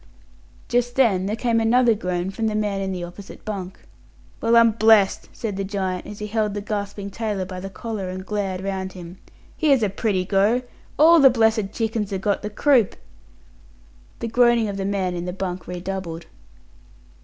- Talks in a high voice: Yes, high, 205 Hz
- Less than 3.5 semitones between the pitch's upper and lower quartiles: Yes, average, 3.0 semitones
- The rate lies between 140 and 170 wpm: No, average, 185 wpm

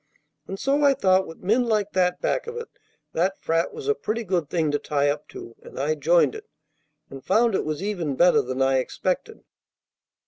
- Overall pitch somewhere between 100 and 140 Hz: No, medium, 185 Hz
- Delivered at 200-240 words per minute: Yes, fast, 205 wpm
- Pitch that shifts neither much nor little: No, wide, 7.3 semitones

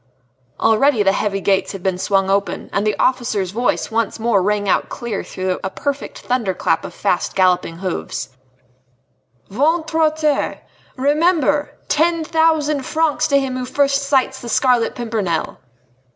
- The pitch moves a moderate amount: No, wide, 6.6 semitones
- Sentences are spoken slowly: No, average, 150 wpm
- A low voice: No, high, 240 Hz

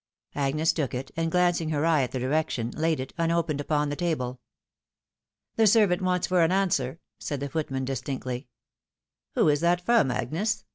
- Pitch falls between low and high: Yes, medium, 155 Hz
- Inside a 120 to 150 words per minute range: No, average, 185 wpm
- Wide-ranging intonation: No, average, 4.5 semitones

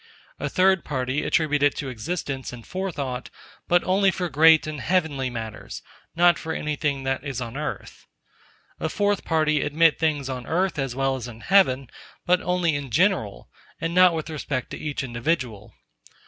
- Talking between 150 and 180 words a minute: Yes, average, 170 wpm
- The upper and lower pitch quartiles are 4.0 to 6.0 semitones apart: Yes, average, 4.4 semitones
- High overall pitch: No, medium, 150 Hz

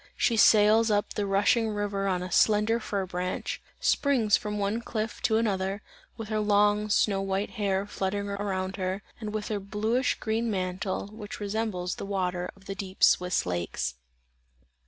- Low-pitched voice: No, high, 205 Hz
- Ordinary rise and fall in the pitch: No, narrow, 2.0 semitones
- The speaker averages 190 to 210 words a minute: No, average, 165 wpm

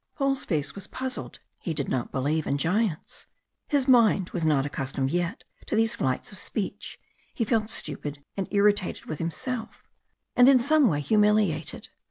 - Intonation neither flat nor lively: No, wide, 7.3 semitones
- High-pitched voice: Yes, high, 195 Hz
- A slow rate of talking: No, average, 165 wpm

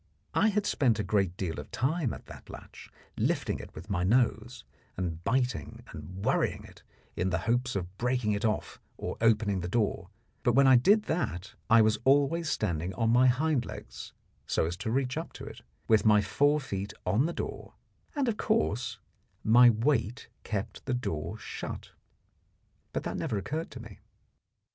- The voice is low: Yes, low, 115 Hz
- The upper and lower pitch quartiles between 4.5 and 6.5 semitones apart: Yes, average, 5.2 semitones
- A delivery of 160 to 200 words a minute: Yes, average, 180 wpm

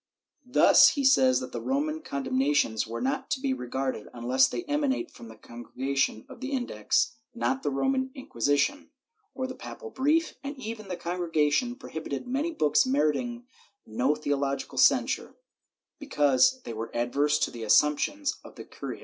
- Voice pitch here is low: No, medium, 175 Hz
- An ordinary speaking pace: Yes, average, 160 wpm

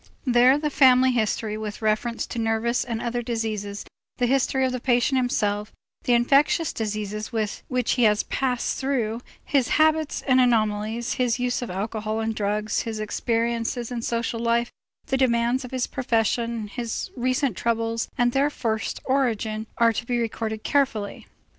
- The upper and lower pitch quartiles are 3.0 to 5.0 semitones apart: No, narrow, 2.5 semitones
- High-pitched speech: Yes, high, 235 Hz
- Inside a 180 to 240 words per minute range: No, average, 160 wpm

